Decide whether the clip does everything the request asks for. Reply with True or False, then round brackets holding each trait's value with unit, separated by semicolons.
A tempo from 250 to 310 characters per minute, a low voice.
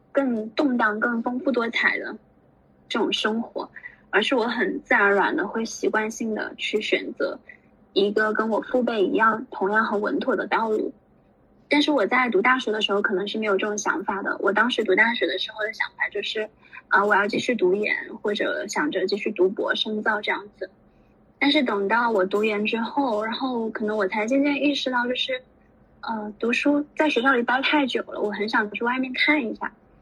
False (285 characters per minute; 225 Hz)